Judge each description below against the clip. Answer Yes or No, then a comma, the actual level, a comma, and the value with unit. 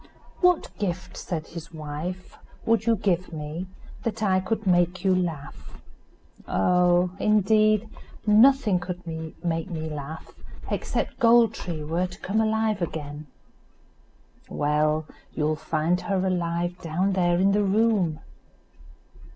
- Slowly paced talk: Yes, slow, 125 wpm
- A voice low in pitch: No, medium, 180 Hz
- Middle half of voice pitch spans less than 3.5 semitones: No, average, 4.2 semitones